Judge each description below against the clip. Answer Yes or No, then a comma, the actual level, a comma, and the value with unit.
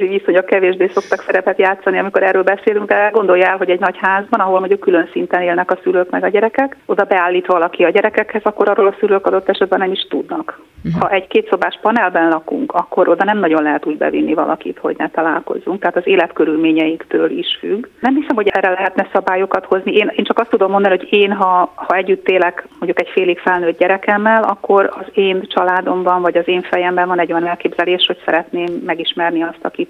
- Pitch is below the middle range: No, high, 190 Hz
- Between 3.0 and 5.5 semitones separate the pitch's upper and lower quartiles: No, narrow, 2.6 semitones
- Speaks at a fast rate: Yes, fast, 205 wpm